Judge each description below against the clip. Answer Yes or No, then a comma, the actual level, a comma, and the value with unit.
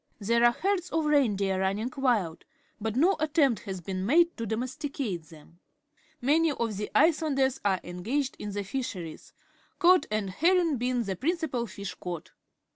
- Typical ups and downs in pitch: No, wide, 7.2 semitones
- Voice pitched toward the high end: Yes, high, 240 Hz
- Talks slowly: No, average, 165 wpm